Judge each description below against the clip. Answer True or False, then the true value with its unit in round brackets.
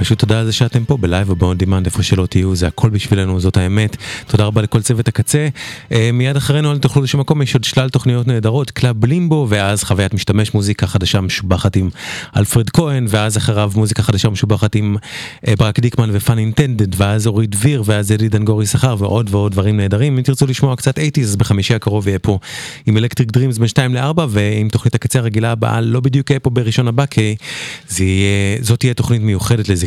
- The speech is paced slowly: False (165 wpm)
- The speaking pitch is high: False (115 Hz)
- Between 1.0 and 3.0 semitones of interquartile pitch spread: False (3.8 semitones)